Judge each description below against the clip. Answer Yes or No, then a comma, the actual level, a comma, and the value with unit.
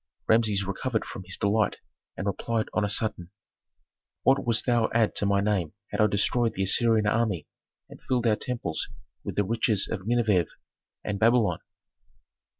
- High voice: No, low, 105 Hz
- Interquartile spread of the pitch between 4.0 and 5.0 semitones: No, average, 2.7 semitones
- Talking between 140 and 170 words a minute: Yes, average, 160 wpm